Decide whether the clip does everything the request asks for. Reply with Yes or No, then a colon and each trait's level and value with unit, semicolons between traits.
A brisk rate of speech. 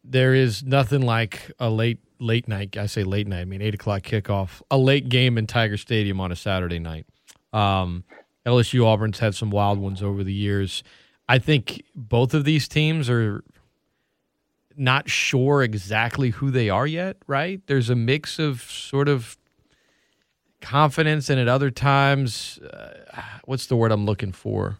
No: average, 170 wpm